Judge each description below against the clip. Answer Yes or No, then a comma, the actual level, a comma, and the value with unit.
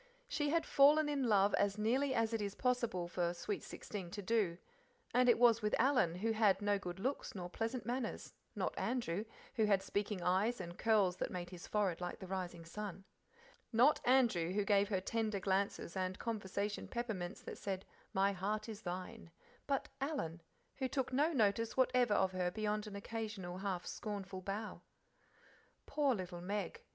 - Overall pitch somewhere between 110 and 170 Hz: No, high, 205 Hz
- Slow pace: No, average, 175 wpm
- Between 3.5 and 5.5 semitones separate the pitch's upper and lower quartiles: Yes, average, 3.8 semitones